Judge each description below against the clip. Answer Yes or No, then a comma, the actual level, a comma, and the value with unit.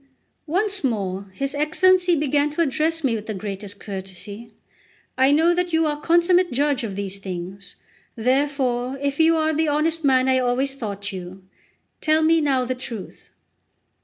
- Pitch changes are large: Yes, wide, 7.0 semitones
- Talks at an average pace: Yes, average, 165 wpm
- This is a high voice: Yes, very high, 270 Hz